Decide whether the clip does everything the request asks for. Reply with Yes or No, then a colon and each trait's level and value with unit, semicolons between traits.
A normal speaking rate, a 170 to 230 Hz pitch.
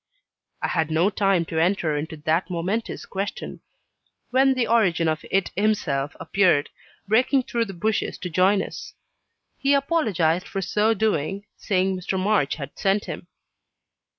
Yes: average, 150 wpm; high, 190 Hz